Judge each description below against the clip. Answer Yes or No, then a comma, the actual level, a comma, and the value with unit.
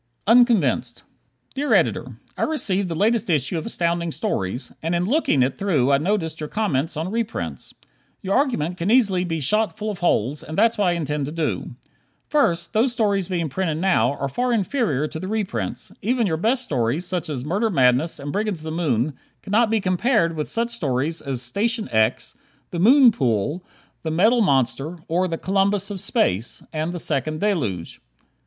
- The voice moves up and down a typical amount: No, wide, 6.2 semitones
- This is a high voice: No, medium, 175 Hz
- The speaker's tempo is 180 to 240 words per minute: Yes, average, 185 wpm